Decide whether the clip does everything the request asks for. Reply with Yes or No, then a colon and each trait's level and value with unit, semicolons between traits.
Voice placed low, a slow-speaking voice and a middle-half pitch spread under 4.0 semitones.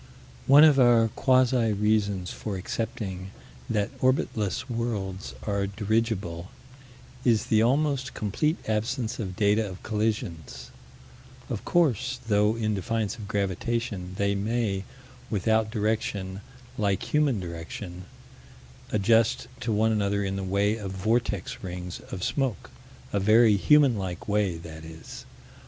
Yes: low, 105 Hz; slow, 125 wpm; average, 3.1 semitones